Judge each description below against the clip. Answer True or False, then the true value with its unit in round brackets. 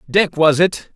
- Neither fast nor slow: True (190 wpm)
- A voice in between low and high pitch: True (165 Hz)